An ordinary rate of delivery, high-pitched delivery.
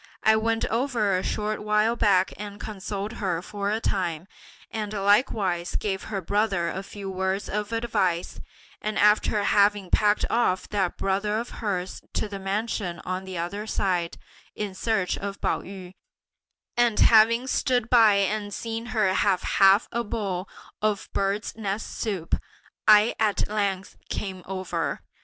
Yes: average, 150 wpm; high, 205 Hz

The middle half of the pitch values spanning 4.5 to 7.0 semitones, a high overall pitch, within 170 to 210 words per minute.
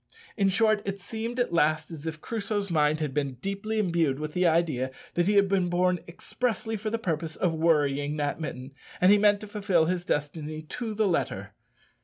No: average, 5.0 semitones; medium, 175 Hz; average, 200 wpm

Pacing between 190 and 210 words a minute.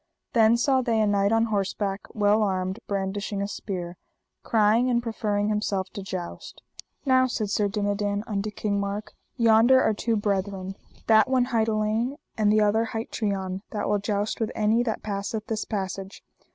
No: average, 170 wpm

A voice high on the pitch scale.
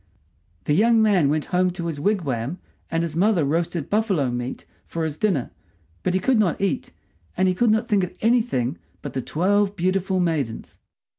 No: medium, 180 Hz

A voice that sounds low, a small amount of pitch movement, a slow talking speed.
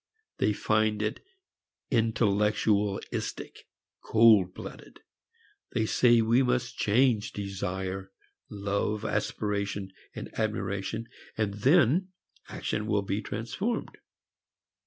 Yes: low, 105 Hz; narrow, 2.3 semitones; slow, 85 wpm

